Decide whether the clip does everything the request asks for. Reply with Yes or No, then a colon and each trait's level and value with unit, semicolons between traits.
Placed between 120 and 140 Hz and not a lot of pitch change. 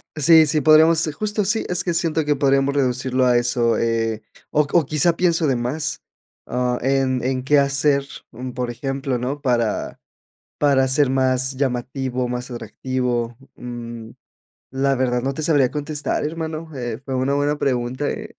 No: low, 135 Hz; average, 3.1 semitones